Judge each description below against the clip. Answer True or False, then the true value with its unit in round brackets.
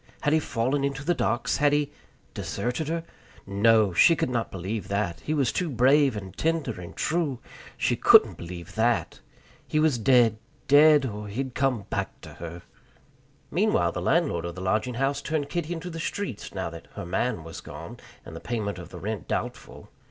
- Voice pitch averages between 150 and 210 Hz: False (120 Hz)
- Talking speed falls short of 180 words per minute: False (190 wpm)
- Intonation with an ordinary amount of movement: False (6.5 semitones)